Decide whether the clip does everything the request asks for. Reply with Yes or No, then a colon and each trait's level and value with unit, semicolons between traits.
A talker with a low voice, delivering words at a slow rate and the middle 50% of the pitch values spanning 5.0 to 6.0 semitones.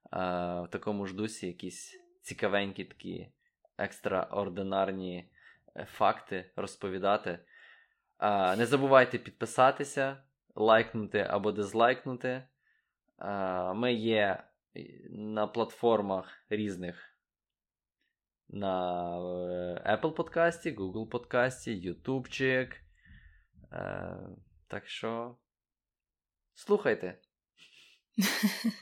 Yes: low, 105 Hz; slow, 60 wpm; wide, 5.6 semitones